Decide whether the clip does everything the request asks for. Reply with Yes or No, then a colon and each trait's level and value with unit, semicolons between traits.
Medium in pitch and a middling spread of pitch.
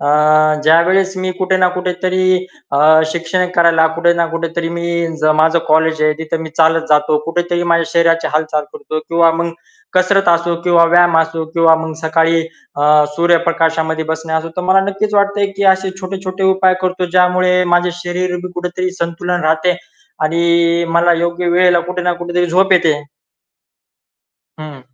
No: medium, 170 Hz; narrow, 1.8 semitones